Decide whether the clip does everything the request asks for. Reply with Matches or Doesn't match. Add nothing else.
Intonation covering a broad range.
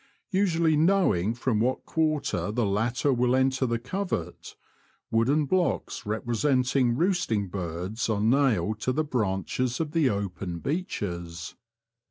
Matches